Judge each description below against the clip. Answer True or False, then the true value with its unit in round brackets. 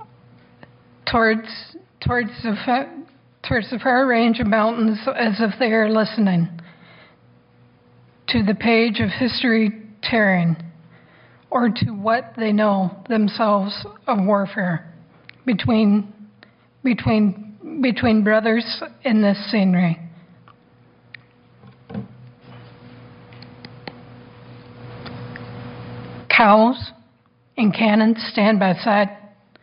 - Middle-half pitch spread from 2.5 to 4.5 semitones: True (3.4 semitones)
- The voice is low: False (215 Hz)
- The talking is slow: True (85 wpm)